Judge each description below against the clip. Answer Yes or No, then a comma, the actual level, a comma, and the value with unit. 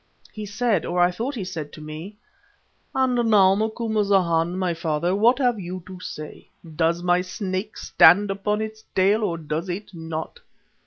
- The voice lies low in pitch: No, medium, 185 Hz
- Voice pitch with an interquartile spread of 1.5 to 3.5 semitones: No, average, 4.0 semitones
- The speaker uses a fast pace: No, average, 165 wpm